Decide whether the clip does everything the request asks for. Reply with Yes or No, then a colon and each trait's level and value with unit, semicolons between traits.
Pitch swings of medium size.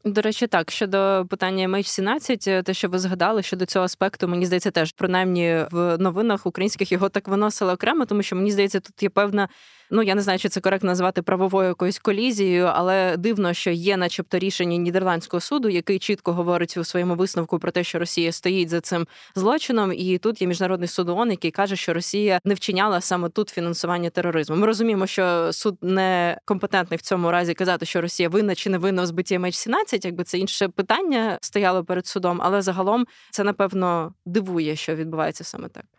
No: narrow, 2.3 semitones